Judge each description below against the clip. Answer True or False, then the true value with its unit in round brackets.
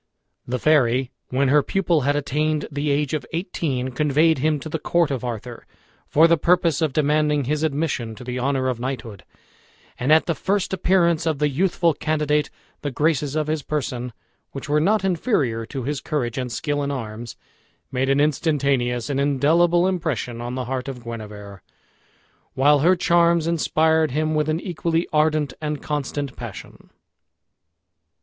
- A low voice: False (145 Hz)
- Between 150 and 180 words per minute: True (165 wpm)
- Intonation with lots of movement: False (3.5 semitones)